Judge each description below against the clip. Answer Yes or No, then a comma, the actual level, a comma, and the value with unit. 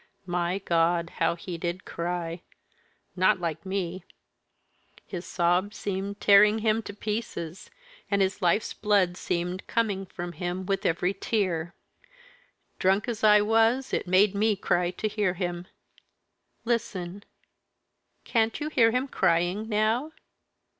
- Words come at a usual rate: No, slow, 130 wpm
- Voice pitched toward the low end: No, high, 190 Hz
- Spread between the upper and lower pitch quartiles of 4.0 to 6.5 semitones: No, average, 3.3 semitones